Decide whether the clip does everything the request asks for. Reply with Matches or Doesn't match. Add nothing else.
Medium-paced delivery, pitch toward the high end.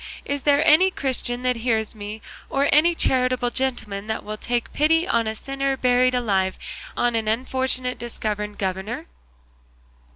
Matches